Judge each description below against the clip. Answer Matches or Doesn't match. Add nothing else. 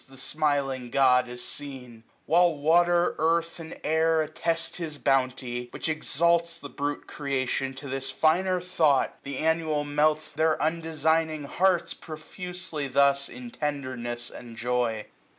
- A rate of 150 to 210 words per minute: Doesn't match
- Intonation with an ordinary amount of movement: Matches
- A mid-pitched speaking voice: Matches